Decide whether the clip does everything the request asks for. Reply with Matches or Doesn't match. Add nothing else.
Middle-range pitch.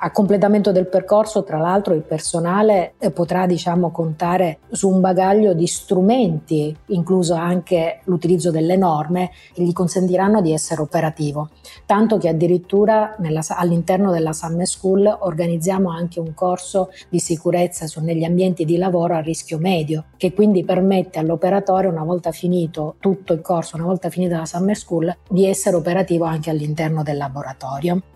Matches